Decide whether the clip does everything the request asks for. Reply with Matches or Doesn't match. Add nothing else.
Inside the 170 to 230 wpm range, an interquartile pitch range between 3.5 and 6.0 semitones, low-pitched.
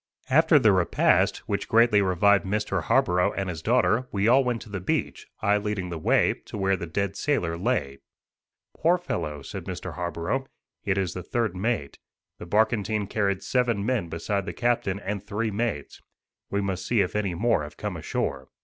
Matches